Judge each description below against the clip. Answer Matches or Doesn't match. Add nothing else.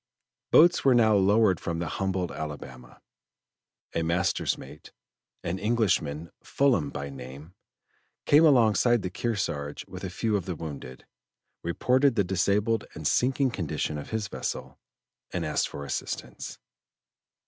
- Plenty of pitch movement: Matches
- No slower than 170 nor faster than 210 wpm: Doesn't match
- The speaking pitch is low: Matches